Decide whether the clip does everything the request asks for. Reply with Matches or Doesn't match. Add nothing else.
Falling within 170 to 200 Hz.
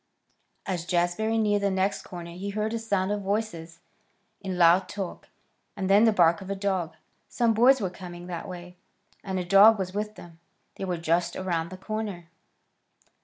Matches